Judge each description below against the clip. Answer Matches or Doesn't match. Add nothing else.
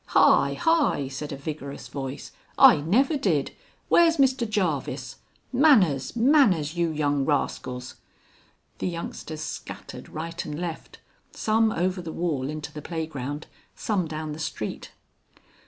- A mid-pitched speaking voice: Matches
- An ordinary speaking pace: Doesn't match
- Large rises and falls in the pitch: Matches